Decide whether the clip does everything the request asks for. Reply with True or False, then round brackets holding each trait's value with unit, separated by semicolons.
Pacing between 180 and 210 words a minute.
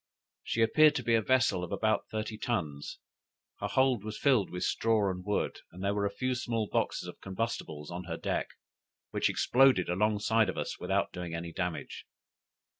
True (185 wpm)